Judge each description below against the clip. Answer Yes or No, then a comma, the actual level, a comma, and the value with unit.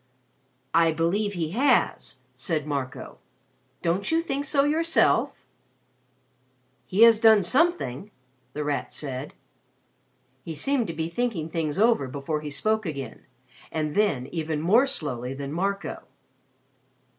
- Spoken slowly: Yes, slow, 125 wpm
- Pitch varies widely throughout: Yes, wide, 6.9 semitones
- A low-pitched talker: No, medium, 165 Hz